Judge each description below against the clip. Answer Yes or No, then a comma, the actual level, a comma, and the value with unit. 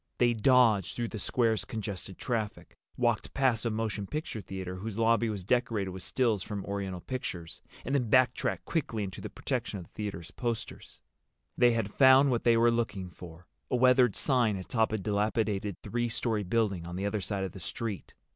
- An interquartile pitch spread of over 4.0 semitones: No, average, 3.4 semitones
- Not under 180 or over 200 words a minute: Yes, average, 185 wpm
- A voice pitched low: Yes, low, 110 Hz